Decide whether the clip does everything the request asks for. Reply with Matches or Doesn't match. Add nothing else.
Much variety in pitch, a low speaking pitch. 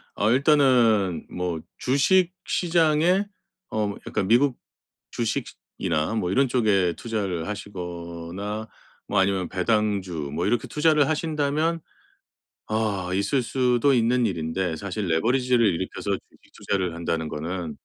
Matches